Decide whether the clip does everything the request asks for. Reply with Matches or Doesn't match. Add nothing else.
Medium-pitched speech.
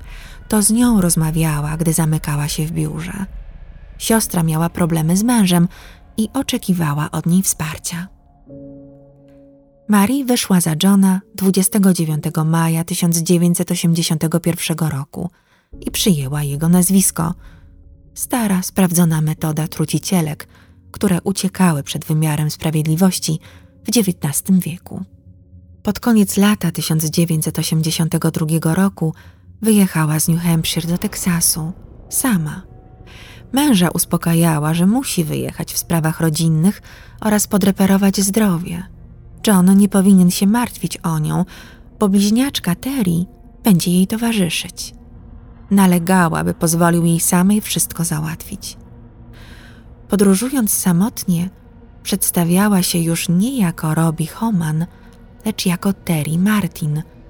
Matches